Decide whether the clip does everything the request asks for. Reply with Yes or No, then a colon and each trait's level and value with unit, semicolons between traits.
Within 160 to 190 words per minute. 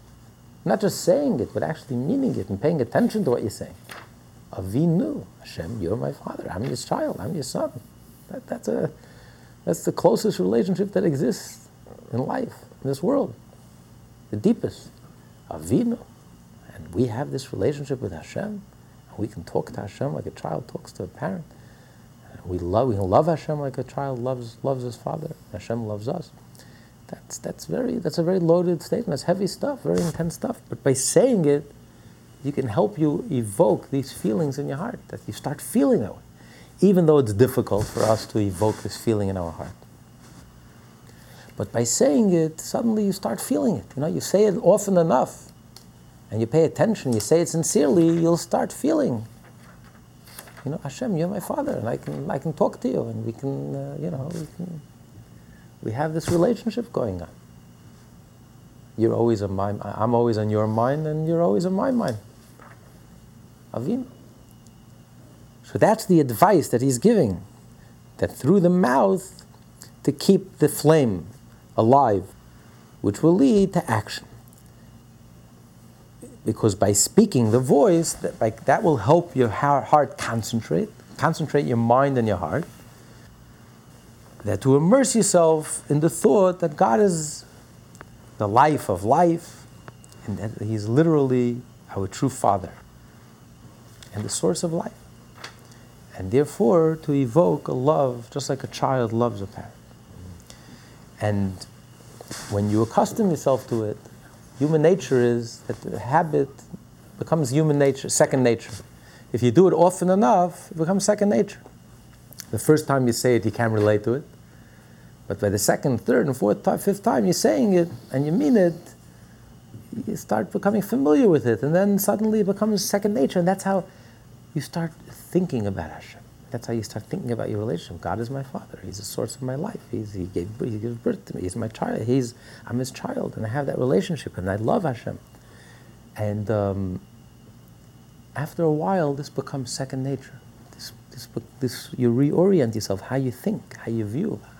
Yes: average, 170 wpm